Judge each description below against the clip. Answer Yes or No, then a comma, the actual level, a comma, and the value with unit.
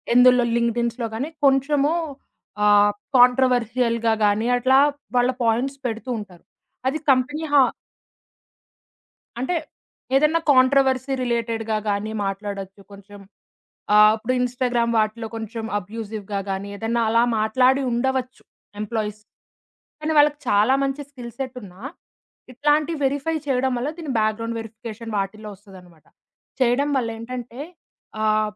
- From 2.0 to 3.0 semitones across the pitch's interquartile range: No, average, 3.5 semitones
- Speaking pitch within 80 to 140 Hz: No, high, 235 Hz